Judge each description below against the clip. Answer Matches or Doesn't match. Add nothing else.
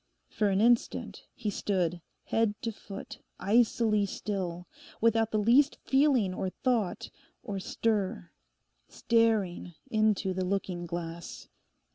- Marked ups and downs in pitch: Doesn't match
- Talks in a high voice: Matches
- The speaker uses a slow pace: Matches